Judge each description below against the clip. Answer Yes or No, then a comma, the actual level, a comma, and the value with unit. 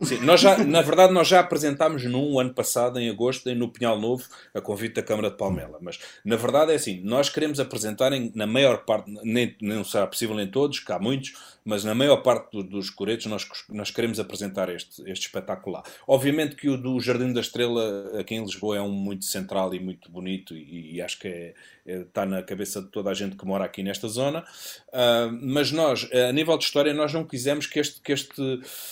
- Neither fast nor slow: No, fast, 225 wpm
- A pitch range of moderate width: No, wide, 5.7 semitones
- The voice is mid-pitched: No, low, 120 Hz